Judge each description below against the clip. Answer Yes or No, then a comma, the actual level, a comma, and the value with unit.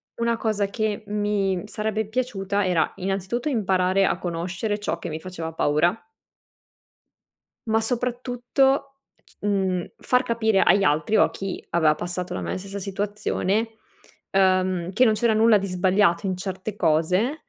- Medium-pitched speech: No, high, 200 Hz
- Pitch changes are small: No, average, 3.2 semitones